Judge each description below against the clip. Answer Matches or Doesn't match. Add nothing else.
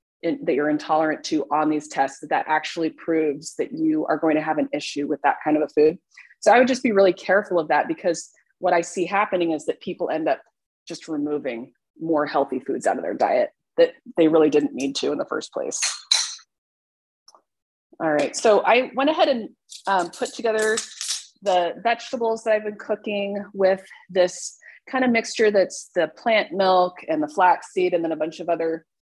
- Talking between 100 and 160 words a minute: Doesn't match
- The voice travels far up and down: Matches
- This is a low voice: Doesn't match